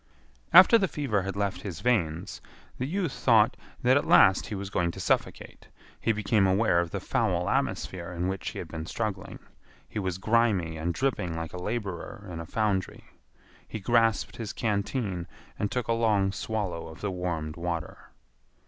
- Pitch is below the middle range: Yes, low, 100 Hz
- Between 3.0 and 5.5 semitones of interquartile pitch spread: Yes, average, 4.4 semitones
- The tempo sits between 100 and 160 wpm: No, average, 175 wpm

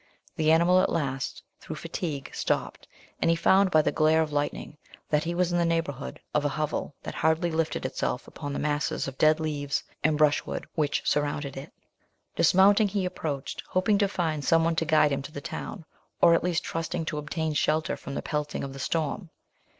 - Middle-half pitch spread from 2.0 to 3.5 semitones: Yes, narrow, 2.4 semitones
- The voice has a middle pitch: Yes, medium, 155 Hz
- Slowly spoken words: No, fast, 205 wpm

